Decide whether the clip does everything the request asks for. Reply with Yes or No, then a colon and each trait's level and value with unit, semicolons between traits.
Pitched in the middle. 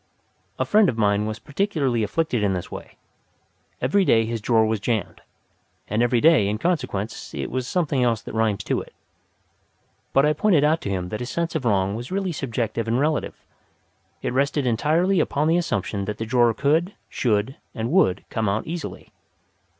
No: low, 120 Hz